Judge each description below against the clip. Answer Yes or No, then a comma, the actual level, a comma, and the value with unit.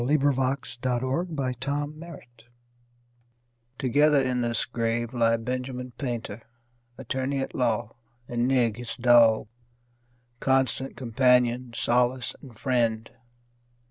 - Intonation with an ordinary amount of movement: No, narrow, 2.1 semitones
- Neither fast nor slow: No, slow, 105 wpm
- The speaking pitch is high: No, low, 125 Hz